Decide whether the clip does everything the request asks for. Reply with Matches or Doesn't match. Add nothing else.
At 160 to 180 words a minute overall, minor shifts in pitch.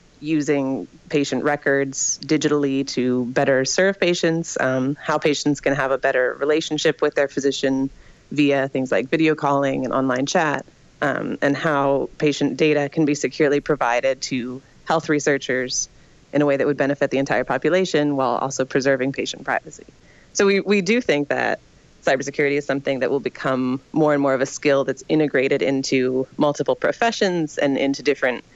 Matches